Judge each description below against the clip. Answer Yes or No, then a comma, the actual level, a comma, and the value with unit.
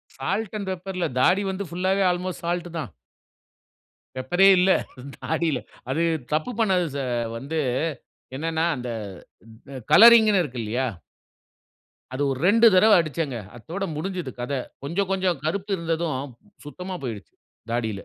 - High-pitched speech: No, medium, 170 Hz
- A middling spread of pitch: No, wide, 5.7 semitones